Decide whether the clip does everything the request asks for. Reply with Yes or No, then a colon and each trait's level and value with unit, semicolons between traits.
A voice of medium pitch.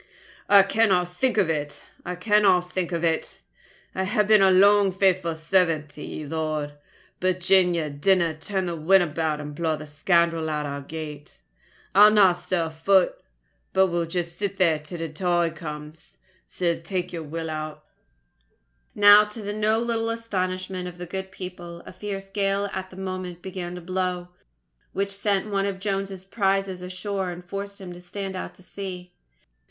Yes: medium, 180 Hz